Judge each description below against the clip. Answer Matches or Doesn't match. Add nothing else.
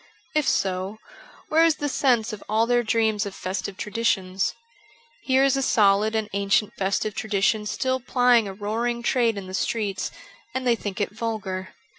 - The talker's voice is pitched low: Doesn't match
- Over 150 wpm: Matches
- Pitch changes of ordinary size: Matches